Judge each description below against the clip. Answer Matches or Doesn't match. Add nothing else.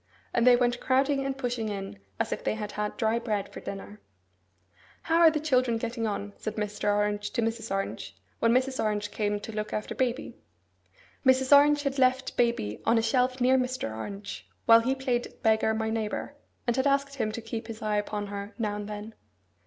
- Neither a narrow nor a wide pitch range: Matches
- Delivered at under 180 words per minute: Doesn't match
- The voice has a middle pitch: Doesn't match